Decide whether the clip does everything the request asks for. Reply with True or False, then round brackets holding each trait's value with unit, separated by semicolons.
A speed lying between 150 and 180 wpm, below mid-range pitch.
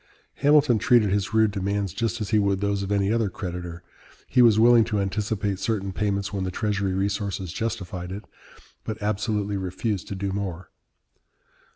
True (170 wpm; 100 Hz)